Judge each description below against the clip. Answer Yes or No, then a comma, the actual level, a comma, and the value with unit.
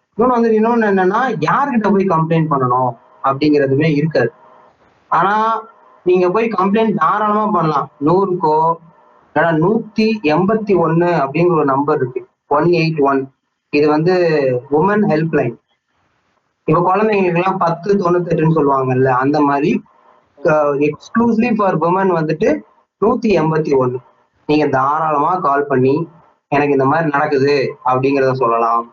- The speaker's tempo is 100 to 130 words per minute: Yes, average, 115 wpm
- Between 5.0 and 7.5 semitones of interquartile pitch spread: Yes, average, 5.3 semitones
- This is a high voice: No, medium, 160 Hz